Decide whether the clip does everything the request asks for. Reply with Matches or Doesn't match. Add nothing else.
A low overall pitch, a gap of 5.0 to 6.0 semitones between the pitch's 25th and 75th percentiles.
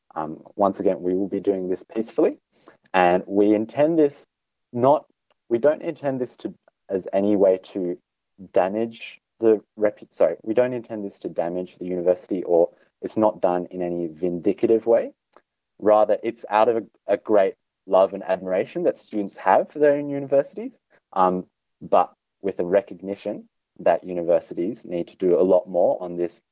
Doesn't match